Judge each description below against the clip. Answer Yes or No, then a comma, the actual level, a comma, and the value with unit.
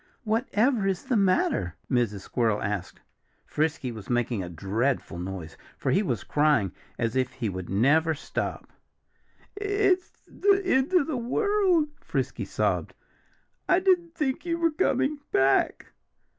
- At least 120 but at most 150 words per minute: Yes, average, 140 wpm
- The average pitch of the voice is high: No, medium, 160 Hz